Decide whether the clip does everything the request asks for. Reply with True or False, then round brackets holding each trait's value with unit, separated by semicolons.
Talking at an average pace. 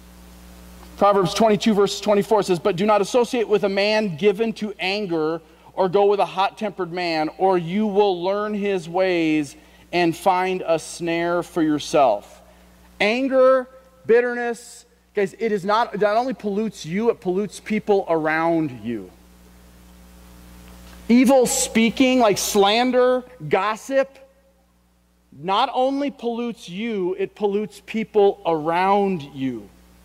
False (125 wpm)